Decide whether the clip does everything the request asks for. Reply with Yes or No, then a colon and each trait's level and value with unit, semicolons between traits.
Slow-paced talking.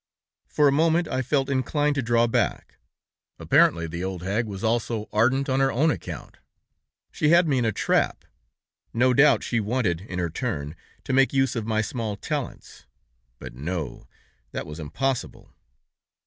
No: average, 165 wpm